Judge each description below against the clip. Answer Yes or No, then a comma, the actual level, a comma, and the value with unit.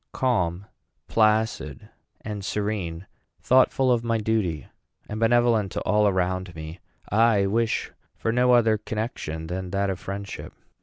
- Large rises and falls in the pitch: No, average, 3.6 semitones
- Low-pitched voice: Yes, low, 105 Hz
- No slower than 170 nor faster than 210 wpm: No, slow, 135 wpm